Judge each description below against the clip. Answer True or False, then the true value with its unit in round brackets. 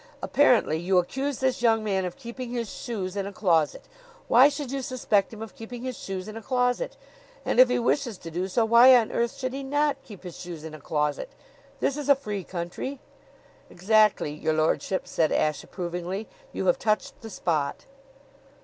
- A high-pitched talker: True (220 Hz)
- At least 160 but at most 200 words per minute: True (195 wpm)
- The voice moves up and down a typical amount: False (6.0 semitones)